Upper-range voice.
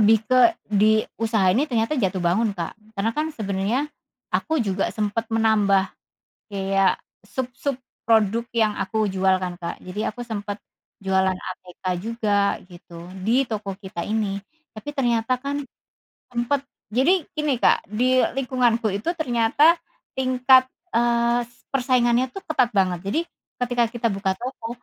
Yes: high, 225 Hz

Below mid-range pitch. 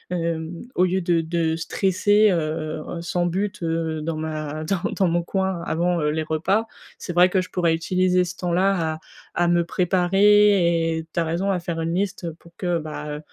No: medium, 170 Hz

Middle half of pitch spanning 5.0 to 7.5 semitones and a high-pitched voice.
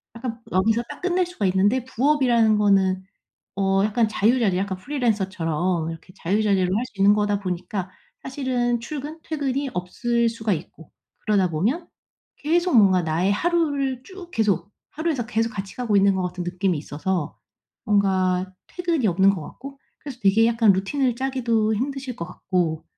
Yes: wide, 5.5 semitones; high, 215 Hz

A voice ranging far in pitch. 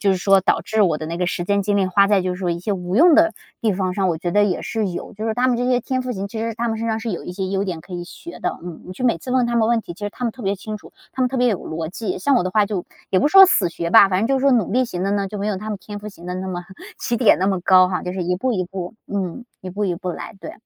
No: average, 3.9 semitones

